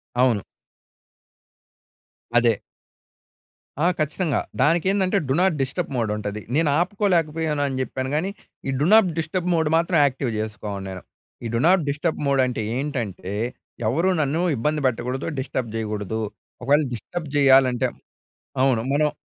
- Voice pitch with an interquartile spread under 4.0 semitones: No, wide, 5.6 semitones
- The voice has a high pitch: No, medium, 140 Hz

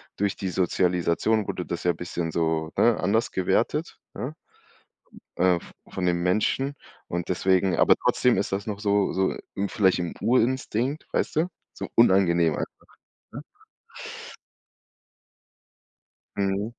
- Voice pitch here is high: No, very low, 95 Hz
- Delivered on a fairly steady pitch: No, average, 3.8 semitones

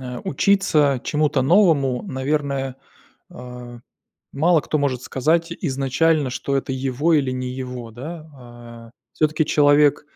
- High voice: No, medium, 140 Hz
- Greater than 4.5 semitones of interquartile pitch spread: No, average, 3.2 semitones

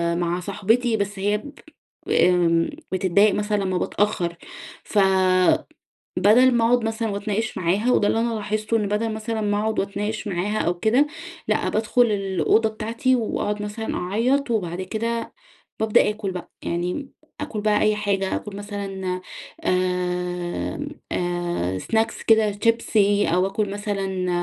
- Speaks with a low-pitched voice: No, high, 205 Hz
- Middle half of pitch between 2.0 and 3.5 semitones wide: Yes, average, 3.0 semitones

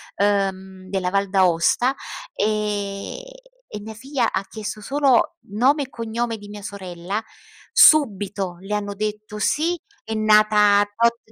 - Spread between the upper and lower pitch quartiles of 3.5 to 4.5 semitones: No, average, 2.7 semitones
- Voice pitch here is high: Yes, high, 210 Hz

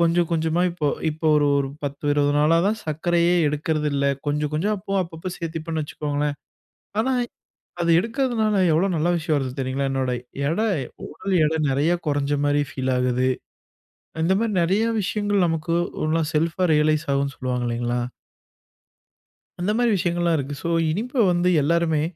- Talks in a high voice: No, medium, 160 Hz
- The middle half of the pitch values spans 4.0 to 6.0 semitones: No, average, 3.3 semitones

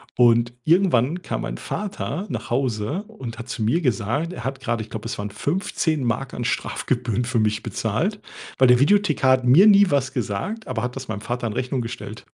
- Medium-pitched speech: No, low, 125 Hz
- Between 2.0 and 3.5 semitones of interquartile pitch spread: No, wide, 5.5 semitones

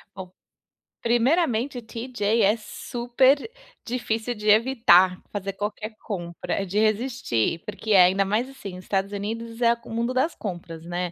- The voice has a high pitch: Yes, high, 220 Hz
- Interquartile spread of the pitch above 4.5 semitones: No, average, 3.7 semitones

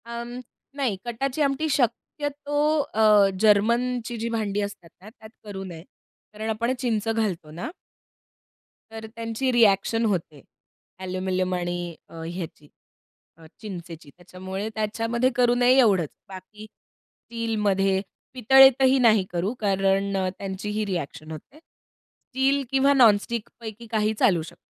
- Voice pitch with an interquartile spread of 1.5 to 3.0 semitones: No, average, 4.0 semitones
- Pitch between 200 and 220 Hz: Yes, high, 215 Hz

